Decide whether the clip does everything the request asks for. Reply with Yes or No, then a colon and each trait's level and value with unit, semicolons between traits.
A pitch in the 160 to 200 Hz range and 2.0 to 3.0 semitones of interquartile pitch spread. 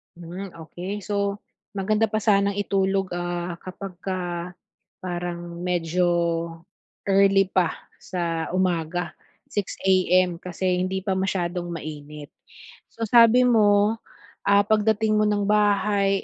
Yes: high, 190 Hz; narrow, 2.6 semitones